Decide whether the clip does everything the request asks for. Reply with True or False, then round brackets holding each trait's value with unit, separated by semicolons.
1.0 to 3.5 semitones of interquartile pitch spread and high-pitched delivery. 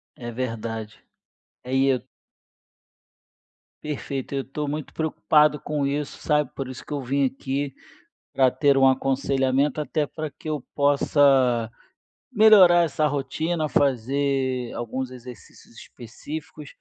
False (2.5 semitones; 140 Hz)